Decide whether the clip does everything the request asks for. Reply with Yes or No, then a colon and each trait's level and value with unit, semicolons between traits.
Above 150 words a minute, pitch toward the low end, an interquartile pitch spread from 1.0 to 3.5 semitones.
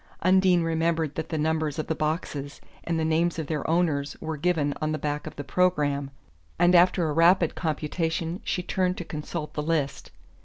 No: average, 190 wpm; medium, 160 Hz; narrow, 2.4 semitones